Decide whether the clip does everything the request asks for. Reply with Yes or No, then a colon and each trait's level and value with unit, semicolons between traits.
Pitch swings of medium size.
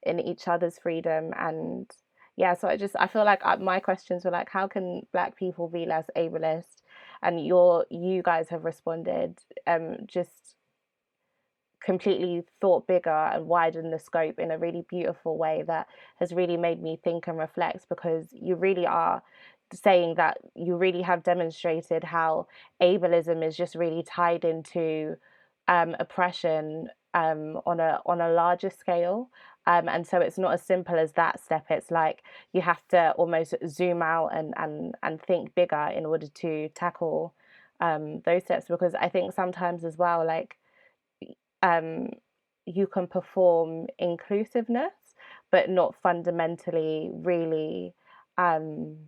No: narrow, 1.7 semitones